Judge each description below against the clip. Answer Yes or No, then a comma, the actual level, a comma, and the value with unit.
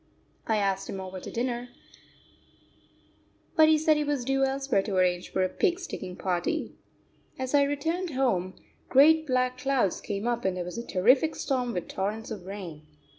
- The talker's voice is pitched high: Yes, high, 240 Hz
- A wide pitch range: Yes, wide, 6.5 semitones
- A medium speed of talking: Yes, average, 180 wpm